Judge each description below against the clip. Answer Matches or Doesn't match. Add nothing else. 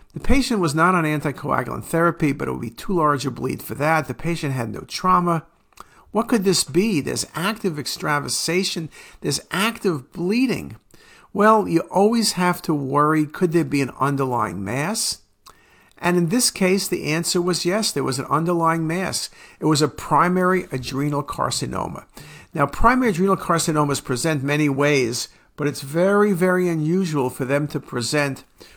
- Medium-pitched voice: Matches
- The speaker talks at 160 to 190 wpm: Matches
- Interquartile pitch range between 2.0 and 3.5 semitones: Doesn't match